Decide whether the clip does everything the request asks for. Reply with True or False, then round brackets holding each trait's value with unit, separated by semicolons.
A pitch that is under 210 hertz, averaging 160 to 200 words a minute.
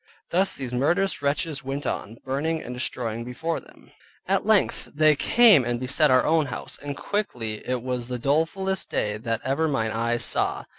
True (135 Hz; 180 wpm)